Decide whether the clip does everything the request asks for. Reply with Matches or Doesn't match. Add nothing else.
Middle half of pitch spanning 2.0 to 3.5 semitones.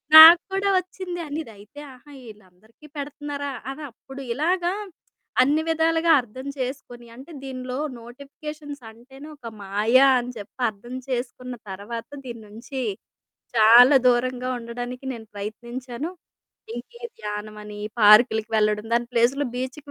Doesn't match